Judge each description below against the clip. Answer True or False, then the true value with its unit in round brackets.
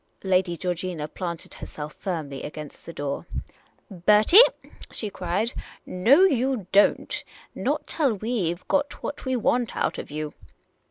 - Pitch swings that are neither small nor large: False (6.0 semitones)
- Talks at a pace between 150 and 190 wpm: True (155 wpm)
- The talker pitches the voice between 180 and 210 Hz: True (185 Hz)